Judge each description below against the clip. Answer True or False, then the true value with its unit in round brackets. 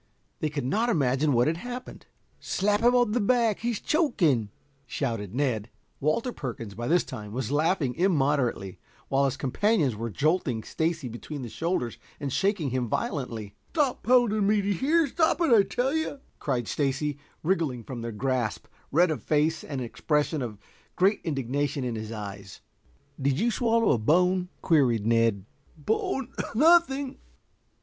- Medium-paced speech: True (155 wpm)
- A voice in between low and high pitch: True (150 Hz)